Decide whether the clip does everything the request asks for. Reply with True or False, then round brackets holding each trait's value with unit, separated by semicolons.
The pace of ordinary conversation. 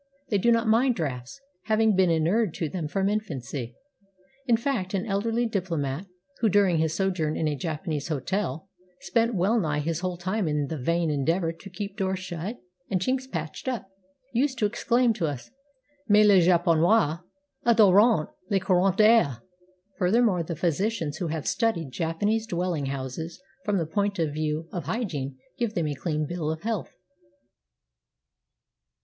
True (160 wpm)